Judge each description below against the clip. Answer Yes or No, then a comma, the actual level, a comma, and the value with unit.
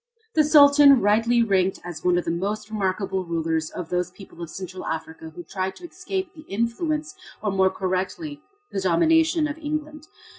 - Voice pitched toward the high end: Yes, high, 200 Hz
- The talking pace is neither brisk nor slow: Yes, average, 175 wpm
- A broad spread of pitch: Yes, wide, 8.7 semitones